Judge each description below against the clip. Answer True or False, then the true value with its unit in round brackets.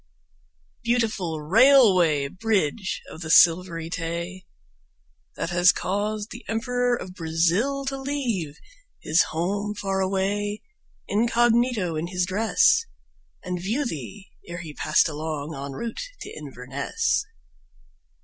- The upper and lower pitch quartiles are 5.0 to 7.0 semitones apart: True (5.4 semitones)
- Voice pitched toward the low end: False (185 Hz)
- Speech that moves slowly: True (115 wpm)